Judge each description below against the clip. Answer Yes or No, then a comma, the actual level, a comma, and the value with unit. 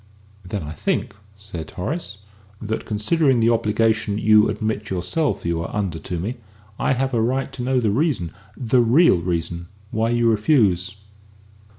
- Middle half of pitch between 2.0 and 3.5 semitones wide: No, average, 4.9 semitones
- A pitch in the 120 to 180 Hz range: No, low, 110 Hz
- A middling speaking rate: Yes, average, 160 wpm